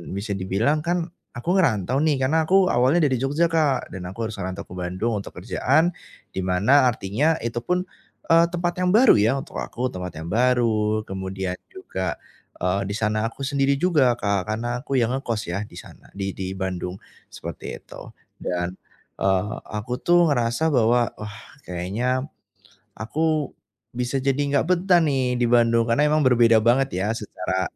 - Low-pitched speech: Yes, low, 120 Hz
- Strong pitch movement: Yes, wide, 6.1 semitones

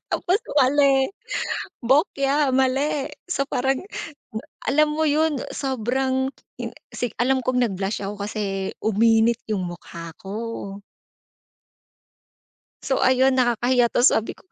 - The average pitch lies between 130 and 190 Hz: No, very high, 255 Hz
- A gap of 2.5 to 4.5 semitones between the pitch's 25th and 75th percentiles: Yes, average, 3.6 semitones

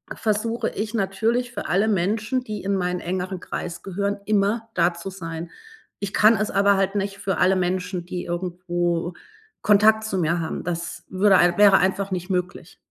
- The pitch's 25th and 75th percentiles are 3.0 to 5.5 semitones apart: No, narrow, 2.6 semitones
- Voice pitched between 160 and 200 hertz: Yes, high, 190 Hz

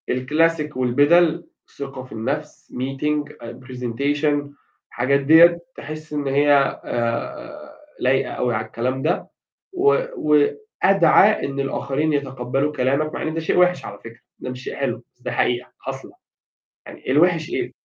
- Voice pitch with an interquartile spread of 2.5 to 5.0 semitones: Yes, average, 3.5 semitones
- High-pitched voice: No, medium, 145 Hz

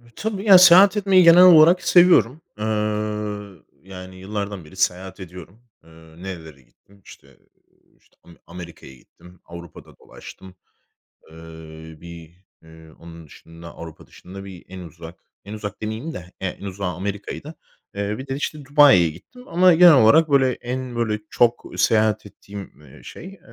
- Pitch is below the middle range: Yes, low, 100 Hz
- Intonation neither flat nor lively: No, wide, 7.7 semitones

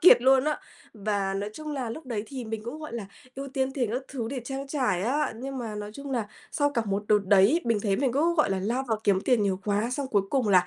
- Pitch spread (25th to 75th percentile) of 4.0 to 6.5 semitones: Yes, average, 4.8 semitones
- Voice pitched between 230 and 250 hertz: Yes, high, 240 Hz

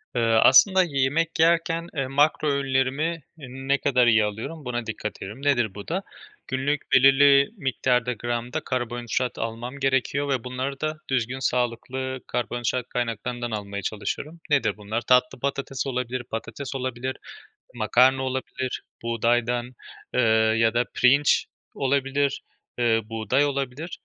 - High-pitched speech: No, low, 130 Hz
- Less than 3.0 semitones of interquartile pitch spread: Yes, narrow, 2.6 semitones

